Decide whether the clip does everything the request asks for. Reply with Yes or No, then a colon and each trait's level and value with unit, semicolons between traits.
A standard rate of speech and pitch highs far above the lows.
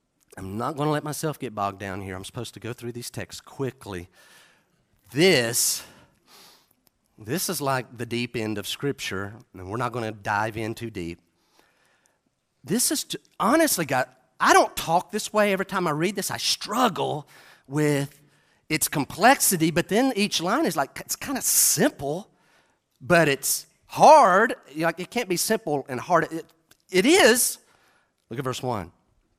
Yes: average, 170 wpm; wide, 7.0 semitones